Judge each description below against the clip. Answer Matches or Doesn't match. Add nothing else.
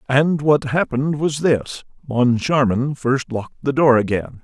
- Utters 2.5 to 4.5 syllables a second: Matches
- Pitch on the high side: Doesn't match